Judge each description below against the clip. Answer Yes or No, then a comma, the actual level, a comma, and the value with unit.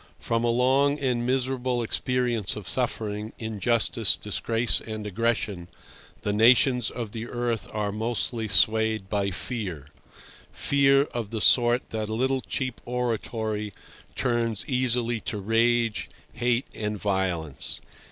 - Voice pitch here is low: Yes, low, 115 Hz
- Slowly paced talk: Yes, slow, 125 wpm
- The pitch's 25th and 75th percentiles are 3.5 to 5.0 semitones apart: No, narrow, 2.6 semitones